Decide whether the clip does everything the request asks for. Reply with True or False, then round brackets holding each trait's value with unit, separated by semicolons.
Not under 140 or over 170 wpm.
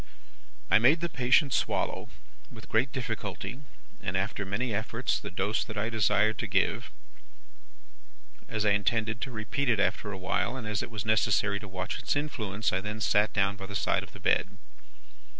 False (185 wpm)